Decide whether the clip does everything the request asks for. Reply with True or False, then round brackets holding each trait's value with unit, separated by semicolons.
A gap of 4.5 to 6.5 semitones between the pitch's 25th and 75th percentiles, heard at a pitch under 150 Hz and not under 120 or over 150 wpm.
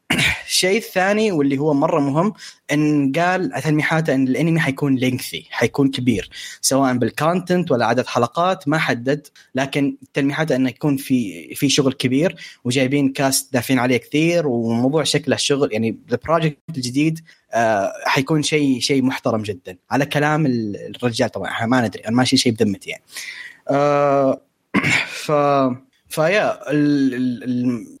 False (2.9 semitones; 140 Hz; 130 wpm)